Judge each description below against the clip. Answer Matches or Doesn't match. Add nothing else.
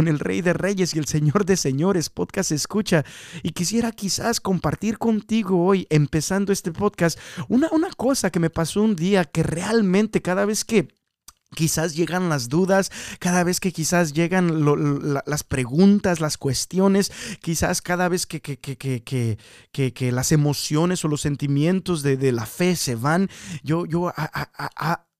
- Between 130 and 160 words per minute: Doesn't match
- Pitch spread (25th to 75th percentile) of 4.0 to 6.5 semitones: Matches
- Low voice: Doesn't match